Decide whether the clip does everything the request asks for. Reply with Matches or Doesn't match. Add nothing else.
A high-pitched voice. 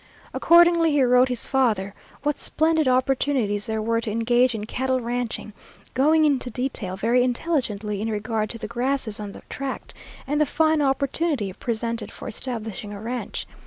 Matches